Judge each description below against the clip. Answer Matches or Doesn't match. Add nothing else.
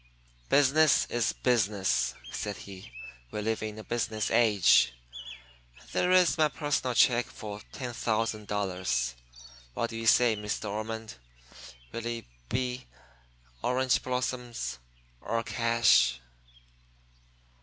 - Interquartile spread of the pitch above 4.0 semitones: Doesn't match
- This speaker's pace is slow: Matches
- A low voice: Matches